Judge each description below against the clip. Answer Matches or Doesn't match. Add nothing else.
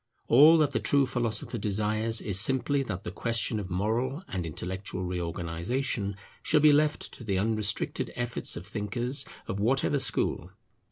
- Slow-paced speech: Doesn't match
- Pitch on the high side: Doesn't match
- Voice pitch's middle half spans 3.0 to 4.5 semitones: Doesn't match